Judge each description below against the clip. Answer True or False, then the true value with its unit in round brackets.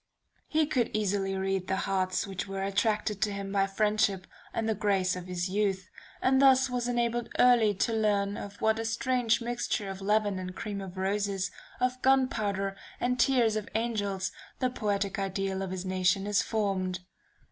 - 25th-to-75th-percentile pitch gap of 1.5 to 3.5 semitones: True (2.8 semitones)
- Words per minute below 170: False (175 wpm)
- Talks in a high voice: True (205 Hz)